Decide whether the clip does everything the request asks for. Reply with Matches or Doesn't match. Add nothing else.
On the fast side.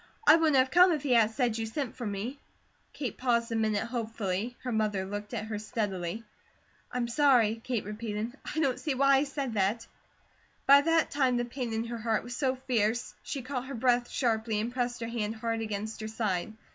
Matches